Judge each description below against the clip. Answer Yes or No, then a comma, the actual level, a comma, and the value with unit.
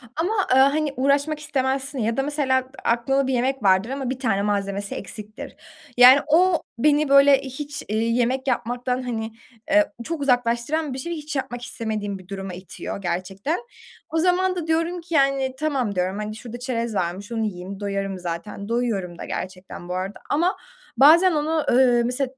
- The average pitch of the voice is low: No, very high, 250 Hz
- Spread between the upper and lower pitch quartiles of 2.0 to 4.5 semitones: No, wide, 5.6 semitones